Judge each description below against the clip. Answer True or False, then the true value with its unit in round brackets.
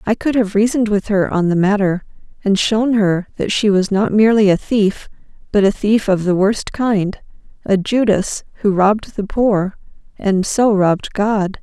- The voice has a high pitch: True (205 Hz)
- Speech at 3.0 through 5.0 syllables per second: True (4.6 syllables/s)